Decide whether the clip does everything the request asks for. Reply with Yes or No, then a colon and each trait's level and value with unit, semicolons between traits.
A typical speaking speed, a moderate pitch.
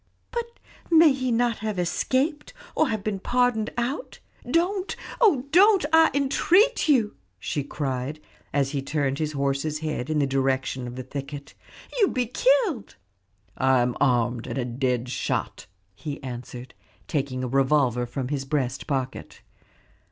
Yes: average, 150 wpm; medium, 150 Hz